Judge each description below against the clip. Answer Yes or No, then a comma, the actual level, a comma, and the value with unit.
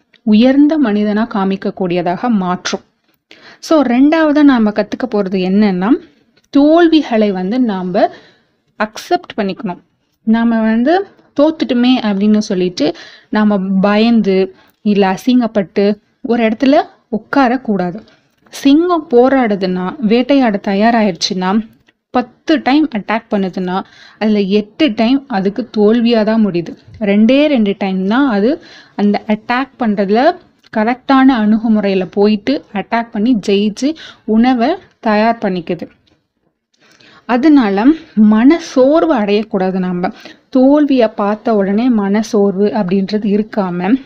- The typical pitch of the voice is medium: No, high, 220 Hz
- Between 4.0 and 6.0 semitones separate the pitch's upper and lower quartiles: Yes, average, 4.4 semitones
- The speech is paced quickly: No, average, 100 wpm